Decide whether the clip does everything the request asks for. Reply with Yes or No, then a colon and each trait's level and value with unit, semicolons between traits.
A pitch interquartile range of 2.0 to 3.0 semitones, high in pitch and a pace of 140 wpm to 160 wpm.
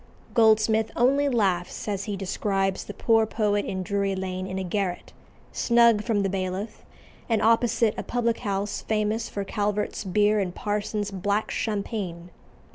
Yes: narrow, 2.4 semitones; high, 205 Hz; average, 150 wpm